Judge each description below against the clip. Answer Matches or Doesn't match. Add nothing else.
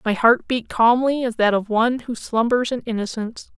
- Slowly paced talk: Doesn't match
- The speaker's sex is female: Matches